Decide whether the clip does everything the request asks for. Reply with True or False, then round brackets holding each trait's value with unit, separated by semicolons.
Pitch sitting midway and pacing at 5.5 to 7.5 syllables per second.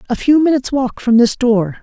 False (245 Hz; 5.6 syllables/s)